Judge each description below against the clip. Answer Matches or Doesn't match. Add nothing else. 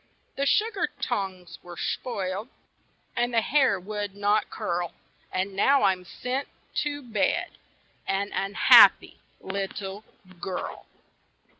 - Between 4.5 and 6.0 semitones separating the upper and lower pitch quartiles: Doesn't match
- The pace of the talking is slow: Matches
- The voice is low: Doesn't match